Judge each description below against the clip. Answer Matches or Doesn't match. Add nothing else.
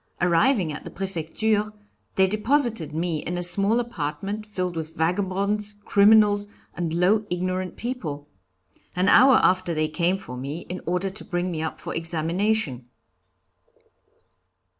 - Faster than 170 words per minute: Doesn't match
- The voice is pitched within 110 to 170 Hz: Doesn't match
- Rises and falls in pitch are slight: Doesn't match